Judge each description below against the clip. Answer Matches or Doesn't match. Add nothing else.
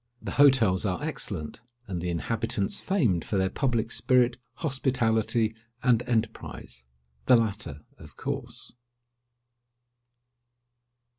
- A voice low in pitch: Matches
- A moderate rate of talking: Doesn't match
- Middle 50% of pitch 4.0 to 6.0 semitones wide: Matches